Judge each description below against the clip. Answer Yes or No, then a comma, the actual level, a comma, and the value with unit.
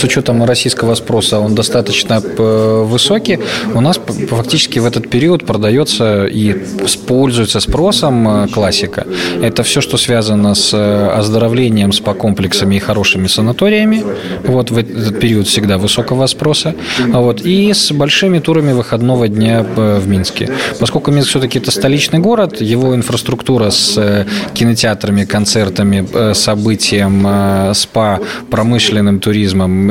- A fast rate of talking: No, average, 120 wpm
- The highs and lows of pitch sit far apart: No, average, 3.7 semitones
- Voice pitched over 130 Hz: No, low, 115 Hz